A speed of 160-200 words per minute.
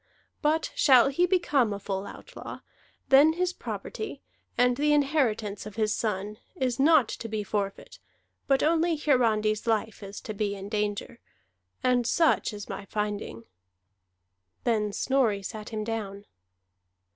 No: average, 140 wpm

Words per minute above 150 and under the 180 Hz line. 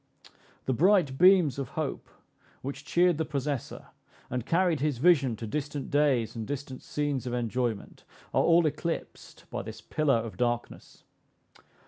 No: average, 145 wpm; medium, 140 Hz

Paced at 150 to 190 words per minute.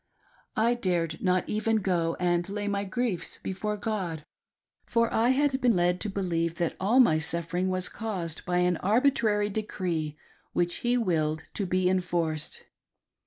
Yes: average, 155 wpm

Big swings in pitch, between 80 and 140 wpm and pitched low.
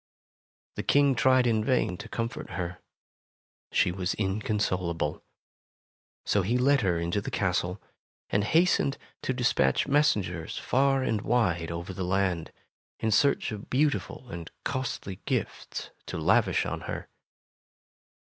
Yes: wide, 6.2 semitones; slow, 135 wpm; low, 105 Hz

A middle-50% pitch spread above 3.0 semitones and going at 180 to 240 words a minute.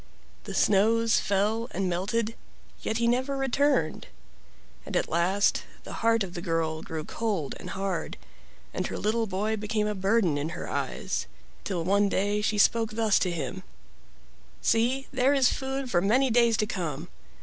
No: average, 3.6 semitones; average, 165 wpm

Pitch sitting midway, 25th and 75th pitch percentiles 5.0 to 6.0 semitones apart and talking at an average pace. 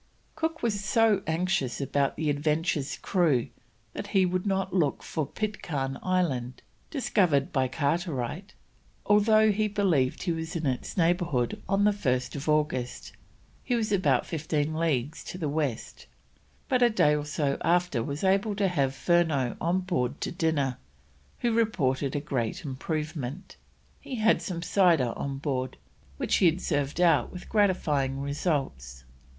Yes: medium, 160 Hz; wide, 5.6 semitones; average, 145 wpm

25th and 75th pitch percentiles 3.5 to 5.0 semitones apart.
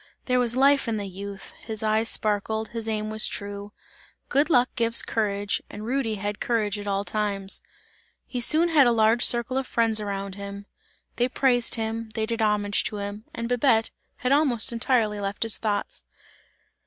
No: average, 2.7 semitones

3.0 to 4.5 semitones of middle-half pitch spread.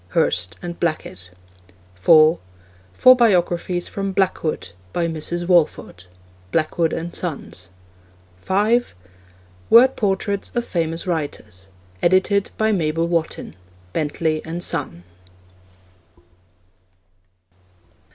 Yes: average, 3.6 semitones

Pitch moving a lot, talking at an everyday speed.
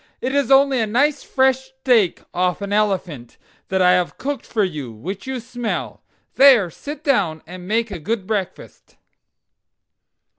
Yes: wide, 6.4 semitones; average, 155 wpm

